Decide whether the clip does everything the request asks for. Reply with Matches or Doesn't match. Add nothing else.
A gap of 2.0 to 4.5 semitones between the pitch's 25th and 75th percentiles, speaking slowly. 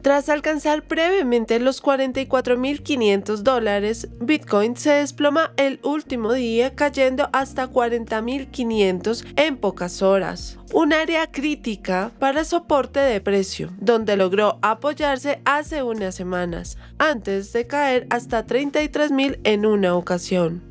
Doesn't match